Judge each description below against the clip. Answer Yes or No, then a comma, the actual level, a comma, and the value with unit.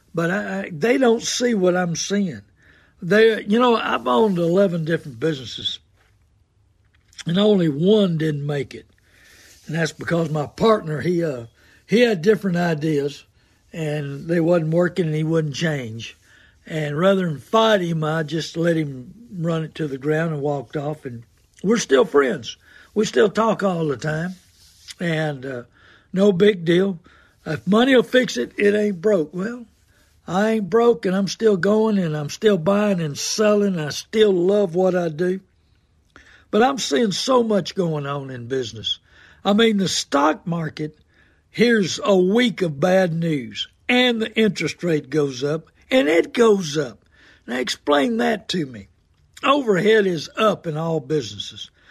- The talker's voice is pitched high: No, medium, 170 Hz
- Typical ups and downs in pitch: No, wide, 6.2 semitones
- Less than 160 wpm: No, average, 165 wpm